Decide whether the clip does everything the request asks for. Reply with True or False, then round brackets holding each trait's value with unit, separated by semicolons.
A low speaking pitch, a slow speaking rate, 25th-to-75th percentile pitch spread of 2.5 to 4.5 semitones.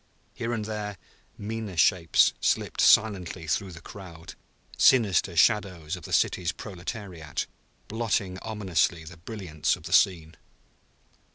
True (95 Hz; 120 wpm; 4.1 semitones)